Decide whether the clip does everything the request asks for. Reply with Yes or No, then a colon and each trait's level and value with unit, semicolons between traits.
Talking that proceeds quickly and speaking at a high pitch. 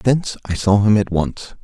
No: fast, 220 wpm; low, 105 Hz